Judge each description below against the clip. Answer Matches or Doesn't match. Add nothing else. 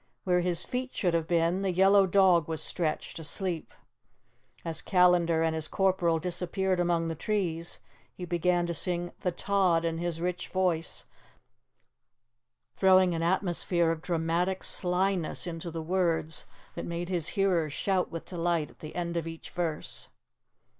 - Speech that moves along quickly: Doesn't match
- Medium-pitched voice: Matches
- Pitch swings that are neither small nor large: Doesn't match